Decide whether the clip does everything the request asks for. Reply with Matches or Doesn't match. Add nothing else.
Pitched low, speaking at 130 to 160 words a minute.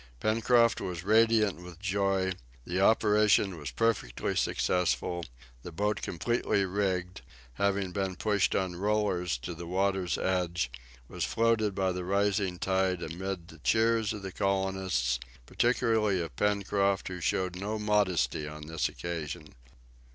Matches